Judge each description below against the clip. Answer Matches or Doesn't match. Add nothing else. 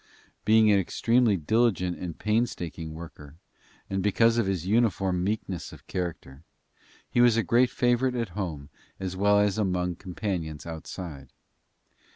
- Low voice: Matches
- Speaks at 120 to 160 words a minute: Matches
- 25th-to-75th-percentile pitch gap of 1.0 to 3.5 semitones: Doesn't match